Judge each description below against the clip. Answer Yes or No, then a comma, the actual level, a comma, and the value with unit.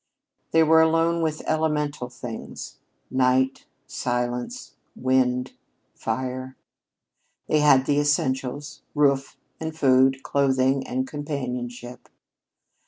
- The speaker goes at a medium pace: No, slow, 100 wpm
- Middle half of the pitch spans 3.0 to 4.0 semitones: No, narrow, 2.6 semitones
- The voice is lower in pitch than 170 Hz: Yes, low, 135 Hz